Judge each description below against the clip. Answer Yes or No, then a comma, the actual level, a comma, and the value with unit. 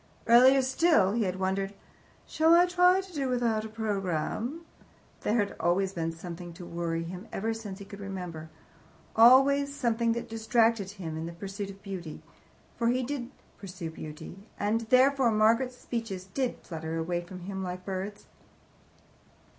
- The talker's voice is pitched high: Yes, high, 205 Hz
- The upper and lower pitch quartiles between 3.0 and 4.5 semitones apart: No, average, 4.9 semitones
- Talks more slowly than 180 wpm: Yes, average, 160 wpm